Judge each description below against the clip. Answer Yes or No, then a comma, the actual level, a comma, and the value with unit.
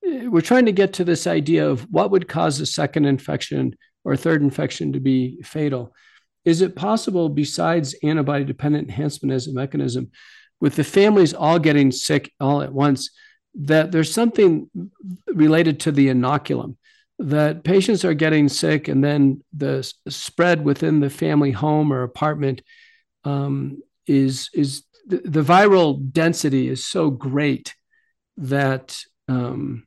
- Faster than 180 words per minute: No, average, 150 wpm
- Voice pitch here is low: No, medium, 150 Hz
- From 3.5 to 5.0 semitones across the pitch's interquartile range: Yes, average, 4.4 semitones